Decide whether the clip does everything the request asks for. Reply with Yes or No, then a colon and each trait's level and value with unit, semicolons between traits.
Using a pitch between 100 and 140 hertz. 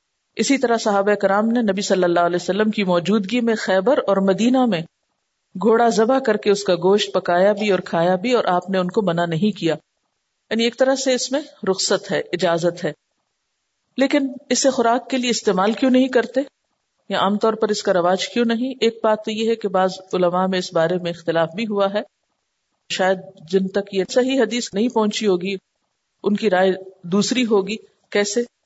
No: high, 205 Hz